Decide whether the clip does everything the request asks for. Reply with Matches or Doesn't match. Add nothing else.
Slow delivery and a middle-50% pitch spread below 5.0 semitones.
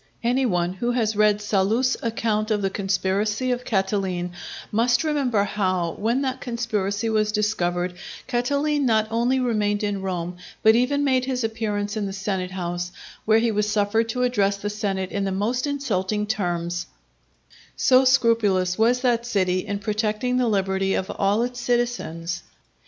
Doesn't match